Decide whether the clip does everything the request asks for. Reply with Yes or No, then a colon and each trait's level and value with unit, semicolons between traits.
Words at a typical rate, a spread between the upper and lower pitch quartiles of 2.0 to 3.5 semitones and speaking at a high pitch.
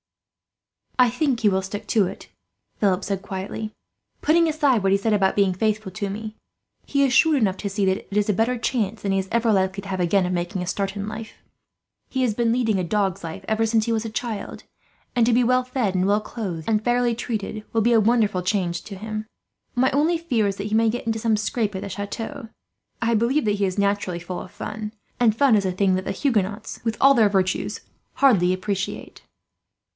No: fast, 230 wpm; average, 3.1 semitones; high, 215 Hz